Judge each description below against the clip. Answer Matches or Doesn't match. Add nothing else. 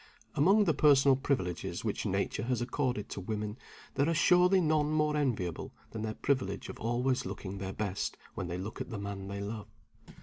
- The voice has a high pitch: Doesn't match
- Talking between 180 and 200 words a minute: Matches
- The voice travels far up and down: Matches